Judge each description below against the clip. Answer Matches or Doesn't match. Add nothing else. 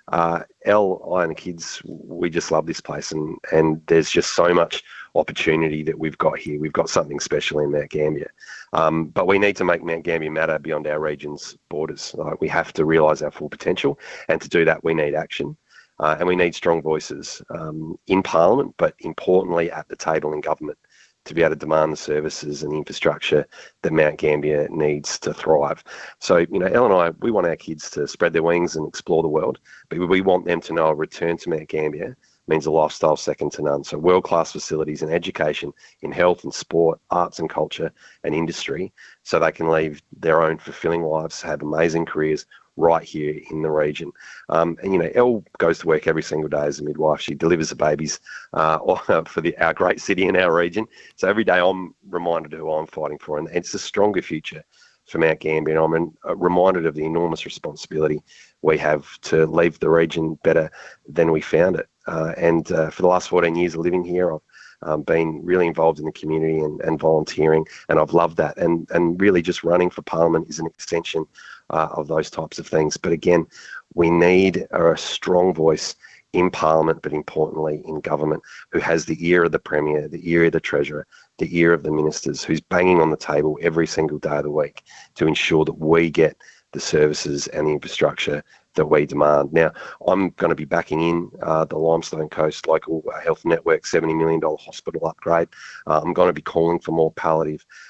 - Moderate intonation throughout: Doesn't match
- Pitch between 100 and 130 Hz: Doesn't match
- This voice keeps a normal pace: Doesn't match